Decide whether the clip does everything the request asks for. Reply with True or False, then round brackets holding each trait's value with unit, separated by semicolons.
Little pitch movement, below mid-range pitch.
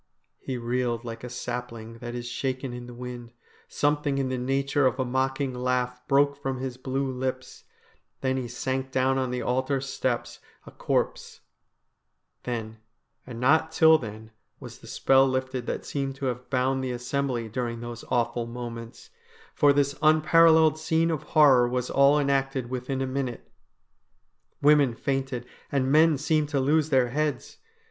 True (2.1 semitones; 130 Hz)